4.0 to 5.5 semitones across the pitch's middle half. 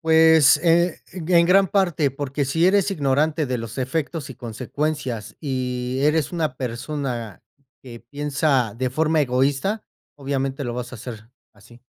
Yes: average, 4.3 semitones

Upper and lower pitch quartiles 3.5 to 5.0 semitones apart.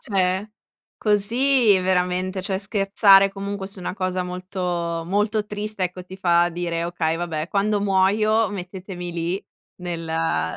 No: narrow, 2.4 semitones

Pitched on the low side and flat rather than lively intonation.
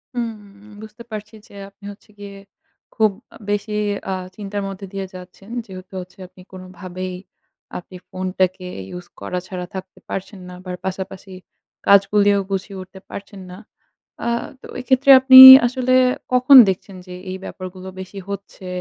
No: high, 195 Hz; narrow, 1.9 semitones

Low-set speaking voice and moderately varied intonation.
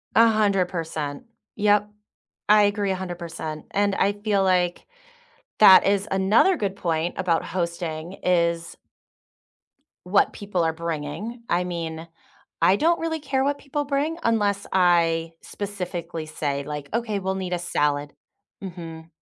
No: medium, 185 Hz; average, 3.8 semitones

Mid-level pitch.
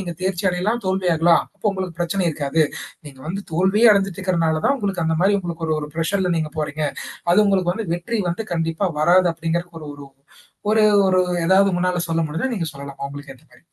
Yes: medium, 175 Hz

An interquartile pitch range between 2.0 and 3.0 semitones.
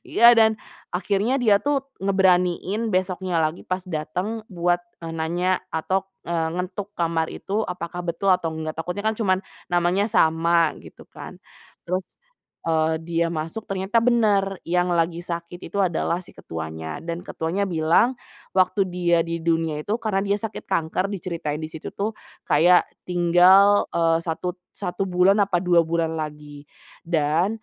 Yes: average, 2.7 semitones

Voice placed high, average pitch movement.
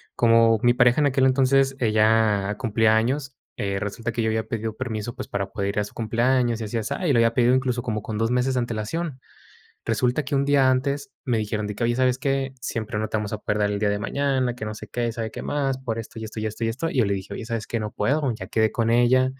No: low, 115 Hz; average, 3.0 semitones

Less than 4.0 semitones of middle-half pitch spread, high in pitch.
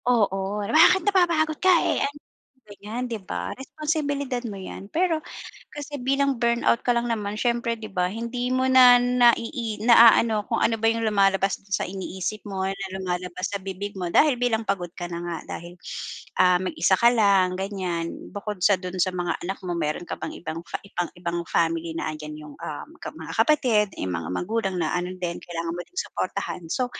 No: average, 5.3 semitones; high, 205 Hz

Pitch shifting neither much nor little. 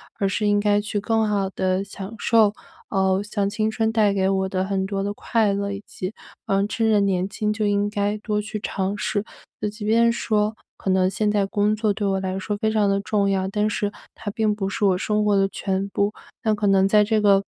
No: narrow, 1.5 semitones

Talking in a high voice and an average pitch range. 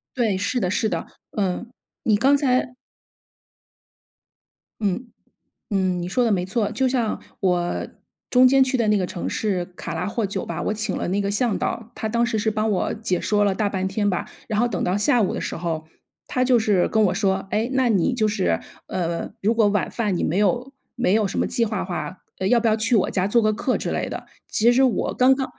Yes: high, 210 Hz; average, 3.8 semitones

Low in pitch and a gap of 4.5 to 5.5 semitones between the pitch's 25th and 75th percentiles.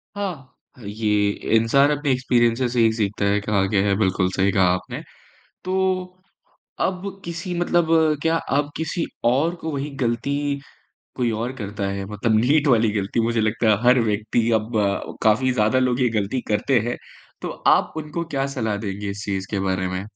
Yes: low, 115 Hz; average, 5.1 semitones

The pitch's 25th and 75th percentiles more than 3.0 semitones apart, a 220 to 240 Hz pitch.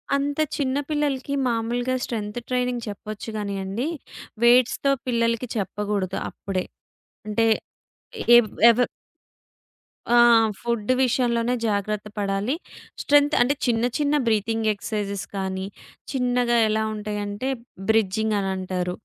Yes: average, 3.4 semitones; high, 225 Hz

